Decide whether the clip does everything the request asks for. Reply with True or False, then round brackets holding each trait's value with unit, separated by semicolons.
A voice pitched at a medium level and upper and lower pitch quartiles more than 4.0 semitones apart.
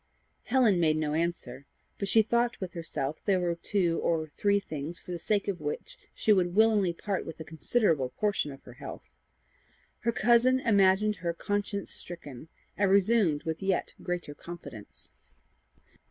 True (180 Hz; 4.4 semitones)